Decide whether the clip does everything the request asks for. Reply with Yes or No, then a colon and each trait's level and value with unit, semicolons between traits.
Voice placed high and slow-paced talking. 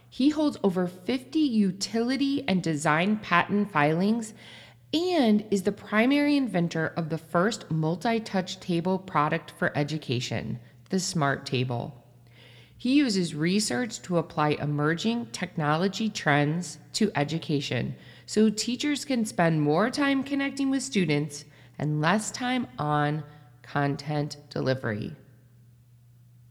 No: medium, 170 Hz; slow, 115 wpm